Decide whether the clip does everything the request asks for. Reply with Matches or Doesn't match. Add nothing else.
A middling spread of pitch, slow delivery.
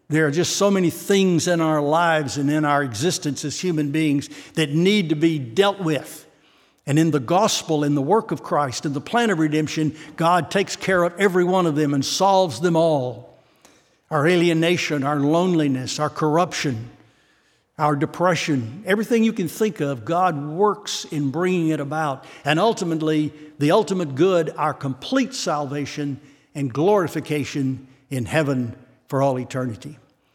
Doesn't match